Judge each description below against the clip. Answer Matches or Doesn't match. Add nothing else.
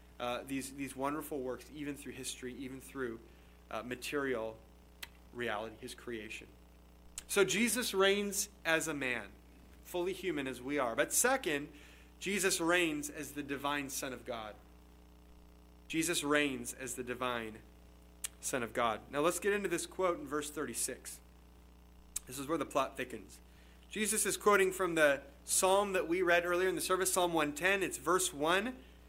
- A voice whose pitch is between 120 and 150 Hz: Matches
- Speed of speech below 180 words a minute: Matches